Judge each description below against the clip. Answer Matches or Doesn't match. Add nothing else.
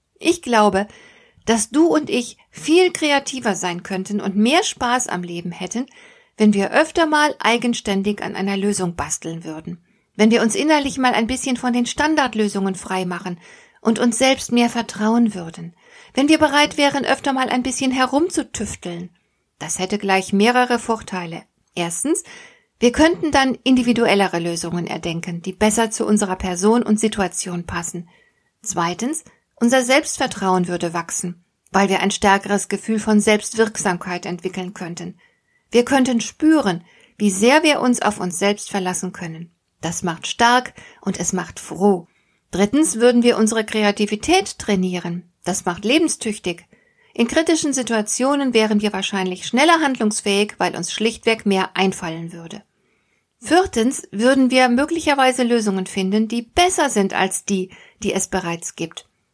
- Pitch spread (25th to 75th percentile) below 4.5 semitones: Doesn't match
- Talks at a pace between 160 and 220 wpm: Doesn't match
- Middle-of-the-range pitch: Doesn't match